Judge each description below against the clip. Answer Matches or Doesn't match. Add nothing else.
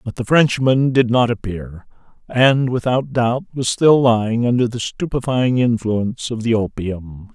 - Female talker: Doesn't match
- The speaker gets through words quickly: Doesn't match